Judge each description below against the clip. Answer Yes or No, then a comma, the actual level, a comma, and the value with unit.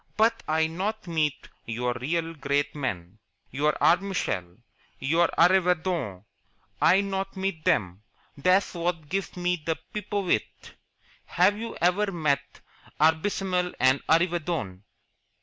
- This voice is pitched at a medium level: Yes, medium, 165 Hz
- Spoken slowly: Yes, slow, 115 wpm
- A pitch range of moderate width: Yes, average, 4.8 semitones